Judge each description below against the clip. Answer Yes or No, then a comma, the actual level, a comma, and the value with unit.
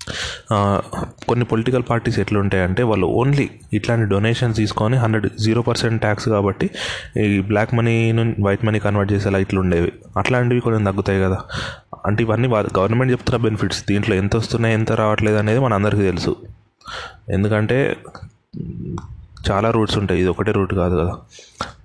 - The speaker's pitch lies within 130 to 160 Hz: No, low, 105 Hz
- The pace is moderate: No, fast, 135 wpm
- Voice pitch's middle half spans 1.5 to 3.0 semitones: Yes, average, 2.7 semitones